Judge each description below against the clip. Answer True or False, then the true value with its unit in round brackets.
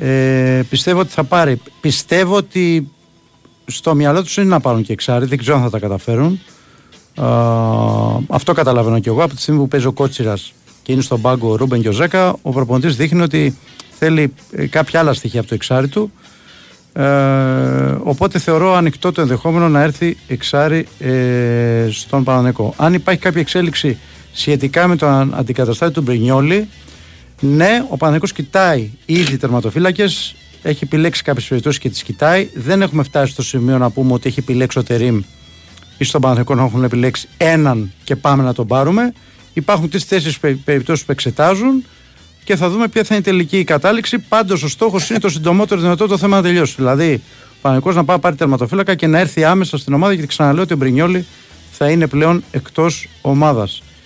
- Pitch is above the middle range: False (145 Hz)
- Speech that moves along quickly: True (180 wpm)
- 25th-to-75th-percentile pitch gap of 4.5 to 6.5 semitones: True (5.2 semitones)